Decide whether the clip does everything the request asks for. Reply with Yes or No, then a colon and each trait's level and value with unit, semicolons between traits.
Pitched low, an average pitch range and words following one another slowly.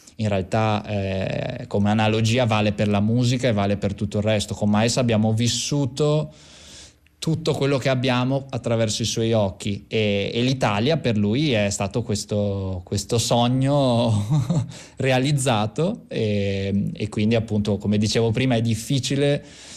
No: low, 115 Hz; average, 3.9 semitones; average, 145 wpm